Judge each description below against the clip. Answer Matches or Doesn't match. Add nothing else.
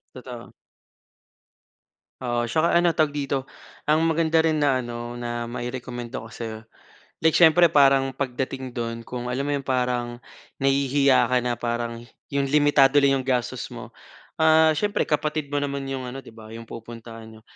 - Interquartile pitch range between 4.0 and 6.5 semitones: Doesn't match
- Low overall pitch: Matches